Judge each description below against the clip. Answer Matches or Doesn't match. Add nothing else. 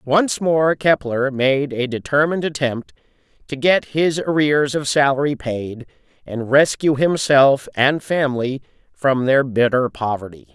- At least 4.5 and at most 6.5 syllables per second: Doesn't match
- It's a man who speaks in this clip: Matches